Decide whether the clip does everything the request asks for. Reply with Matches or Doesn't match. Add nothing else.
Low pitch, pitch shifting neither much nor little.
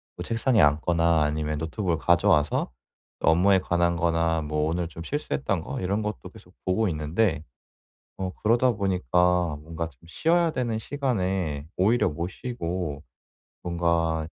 Matches